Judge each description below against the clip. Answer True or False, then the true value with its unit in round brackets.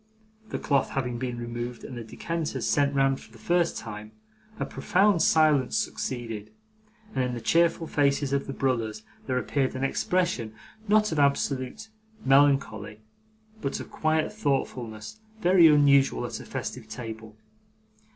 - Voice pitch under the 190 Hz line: True (135 Hz)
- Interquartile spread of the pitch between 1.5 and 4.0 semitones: False (4.8 semitones)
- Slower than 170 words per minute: True (145 wpm)